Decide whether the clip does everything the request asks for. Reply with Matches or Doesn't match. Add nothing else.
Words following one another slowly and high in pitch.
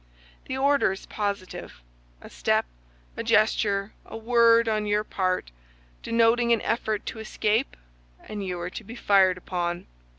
Doesn't match